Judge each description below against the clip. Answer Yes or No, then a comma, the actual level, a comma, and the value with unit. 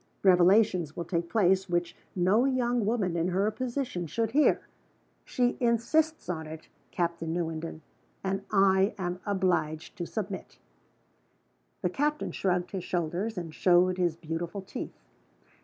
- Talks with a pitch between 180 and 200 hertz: Yes, medium, 185 Hz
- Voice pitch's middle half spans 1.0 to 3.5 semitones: No, average, 4.0 semitones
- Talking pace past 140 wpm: No, slow, 135 wpm